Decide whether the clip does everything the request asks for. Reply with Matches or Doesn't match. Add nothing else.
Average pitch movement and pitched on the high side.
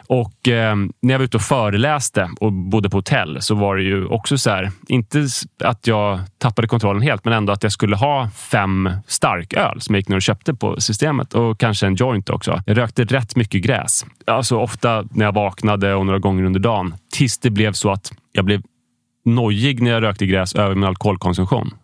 Doesn't match